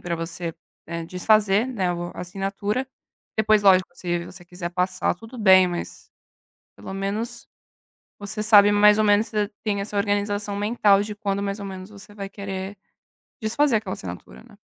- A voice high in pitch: Yes, high, 200 Hz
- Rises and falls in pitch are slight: Yes, narrow, 2.2 semitones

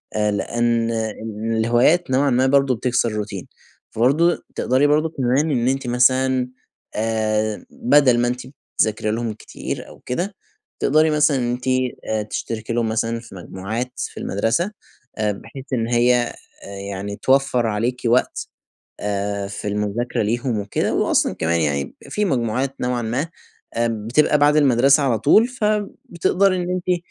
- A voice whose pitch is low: Yes, low, 120 Hz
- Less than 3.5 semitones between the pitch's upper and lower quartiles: No, average, 4.1 semitones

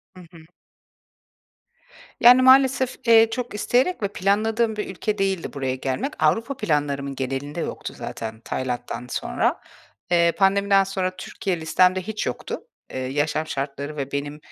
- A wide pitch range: Yes, wide, 7.3 semitones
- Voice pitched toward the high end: No, medium, 180 Hz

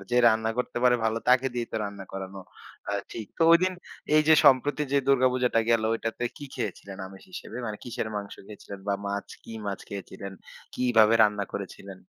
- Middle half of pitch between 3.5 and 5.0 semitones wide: Yes, average, 3.9 semitones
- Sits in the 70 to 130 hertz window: Yes, low, 110 Hz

